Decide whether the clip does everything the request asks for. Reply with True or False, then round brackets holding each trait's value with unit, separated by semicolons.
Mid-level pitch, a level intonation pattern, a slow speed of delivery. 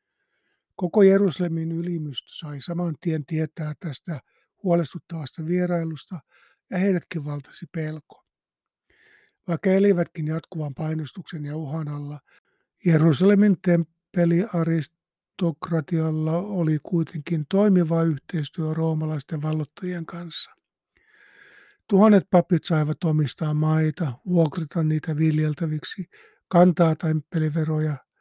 True (165 Hz; 2.3 semitones; 85 wpm)